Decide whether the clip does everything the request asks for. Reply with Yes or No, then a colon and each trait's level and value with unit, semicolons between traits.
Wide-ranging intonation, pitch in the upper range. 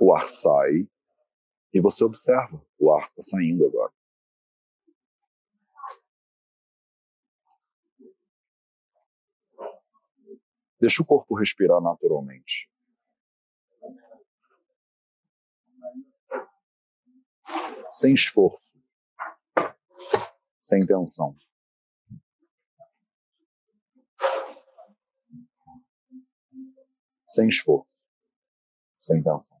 Yes: wide, 7.2 semitones; very high, 265 Hz